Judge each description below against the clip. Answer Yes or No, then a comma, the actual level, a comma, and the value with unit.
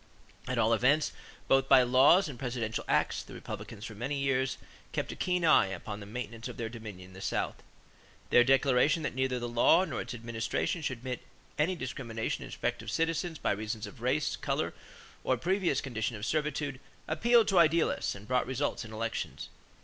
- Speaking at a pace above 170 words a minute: Yes, average, 190 wpm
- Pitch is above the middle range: No, low, 125 Hz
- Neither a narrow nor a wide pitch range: Yes, average, 4.5 semitones